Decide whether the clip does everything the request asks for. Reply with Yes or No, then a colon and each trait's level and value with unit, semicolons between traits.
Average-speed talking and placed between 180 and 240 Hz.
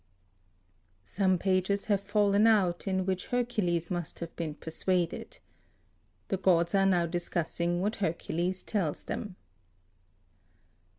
No: slow, 115 wpm; medium, 185 Hz